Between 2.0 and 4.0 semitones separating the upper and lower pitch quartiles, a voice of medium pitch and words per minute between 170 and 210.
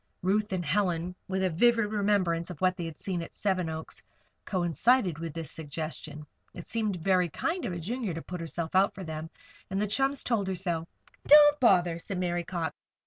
Yes: average, 3.7 semitones; medium, 180 Hz; average, 195 wpm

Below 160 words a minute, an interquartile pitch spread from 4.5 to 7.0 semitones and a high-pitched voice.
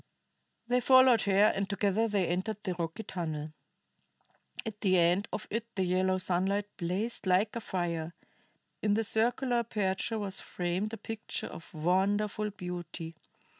No: average, 145 wpm; average, 3.4 semitones; high, 195 Hz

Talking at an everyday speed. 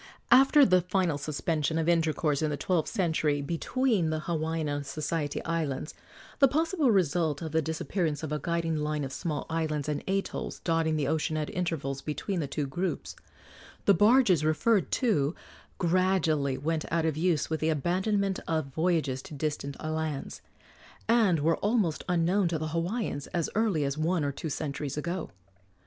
Yes: average, 165 wpm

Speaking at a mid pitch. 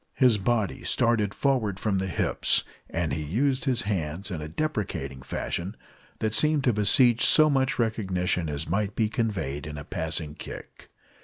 No: low, 105 Hz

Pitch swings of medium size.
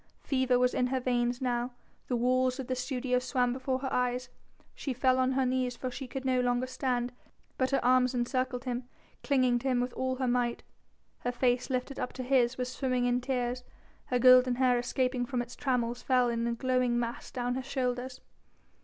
No: narrow, 0.9 semitones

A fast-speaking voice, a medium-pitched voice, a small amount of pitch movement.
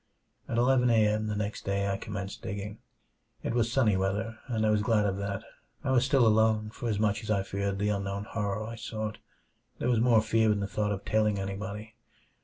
No: fast, 215 wpm; low, 105 Hz; narrow, 2.0 semitones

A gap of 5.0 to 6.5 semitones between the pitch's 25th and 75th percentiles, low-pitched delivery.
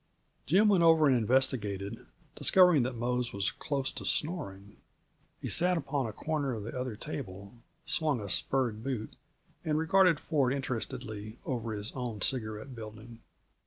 Yes: wide, 5.6 semitones; low, 125 Hz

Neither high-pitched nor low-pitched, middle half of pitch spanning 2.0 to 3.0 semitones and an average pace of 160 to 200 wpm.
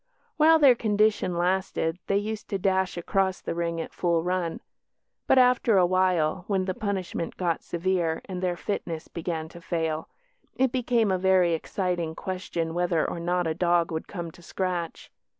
Yes: medium, 180 Hz; narrow, 2.4 semitones; average, 170 wpm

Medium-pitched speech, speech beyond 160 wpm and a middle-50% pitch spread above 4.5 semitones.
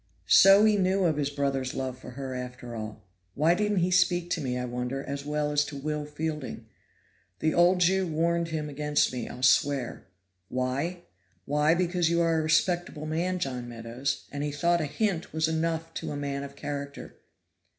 No: medium, 150 Hz; average, 190 wpm; average, 3.9 semitones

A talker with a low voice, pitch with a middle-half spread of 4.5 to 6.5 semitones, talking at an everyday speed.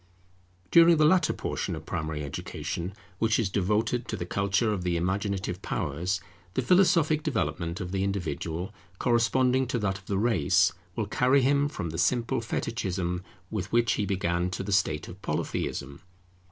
Yes: low, 100 Hz; average, 5.2 semitones; average, 165 wpm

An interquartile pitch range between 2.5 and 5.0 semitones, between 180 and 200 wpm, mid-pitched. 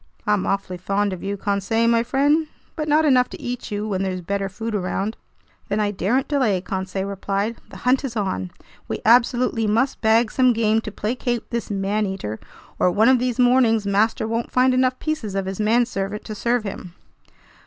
No: average, 3.8 semitones; average, 190 wpm; high, 215 Hz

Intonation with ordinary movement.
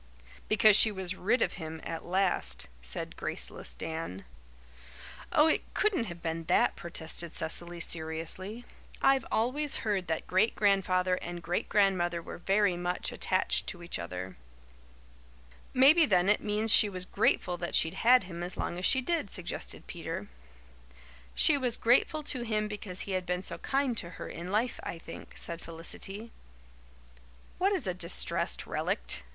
Yes: average, 4.4 semitones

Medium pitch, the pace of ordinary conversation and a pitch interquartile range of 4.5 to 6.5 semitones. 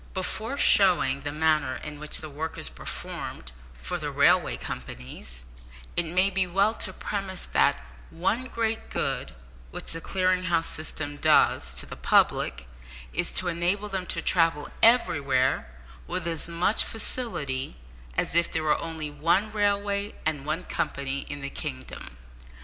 Yes: medium, 165 Hz; average, 150 wpm; average, 5.1 semitones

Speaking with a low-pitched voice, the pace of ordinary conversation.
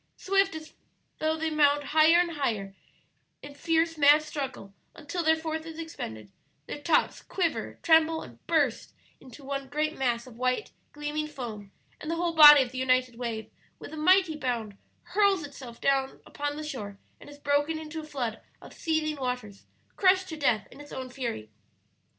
No: very high, 295 Hz; average, 175 wpm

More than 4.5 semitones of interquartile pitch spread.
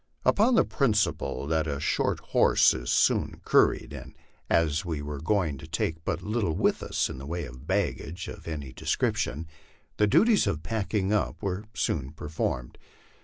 Yes: wide, 5.5 semitones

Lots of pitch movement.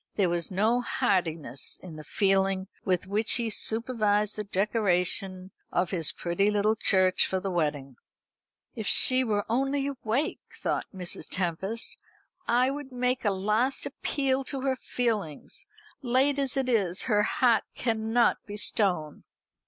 No: average, 4.9 semitones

